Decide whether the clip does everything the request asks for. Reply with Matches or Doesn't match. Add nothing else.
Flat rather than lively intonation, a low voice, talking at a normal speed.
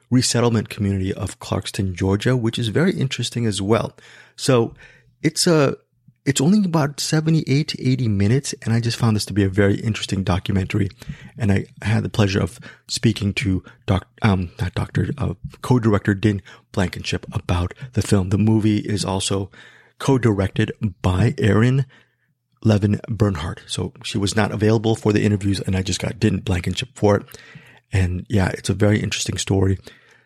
Doesn't match